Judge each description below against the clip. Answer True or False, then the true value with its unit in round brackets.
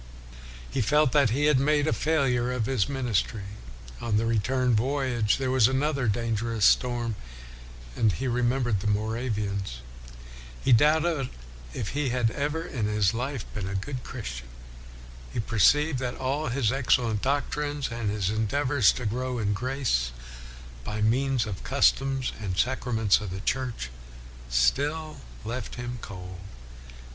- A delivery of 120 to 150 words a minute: True (145 wpm)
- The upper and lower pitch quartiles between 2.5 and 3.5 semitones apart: False (4.1 semitones)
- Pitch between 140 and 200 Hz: False (120 Hz)